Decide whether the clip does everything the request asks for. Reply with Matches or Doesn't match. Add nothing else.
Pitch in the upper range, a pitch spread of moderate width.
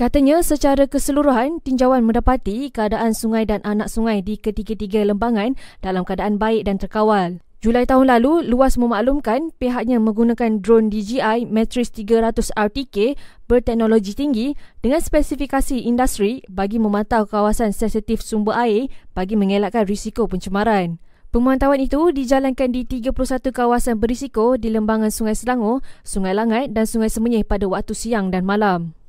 Matches